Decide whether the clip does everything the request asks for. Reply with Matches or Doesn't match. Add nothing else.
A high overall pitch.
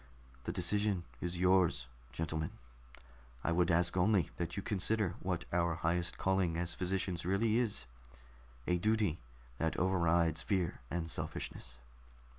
Doesn't match